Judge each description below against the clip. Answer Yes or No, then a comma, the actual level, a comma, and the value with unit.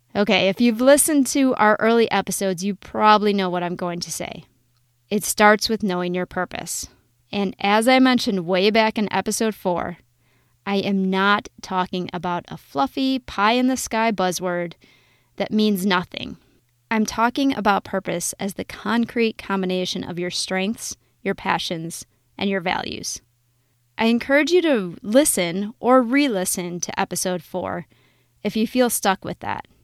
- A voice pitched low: No, high, 195 Hz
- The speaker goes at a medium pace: Yes, average, 160 wpm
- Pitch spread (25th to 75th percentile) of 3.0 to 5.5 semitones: Yes, average, 3.9 semitones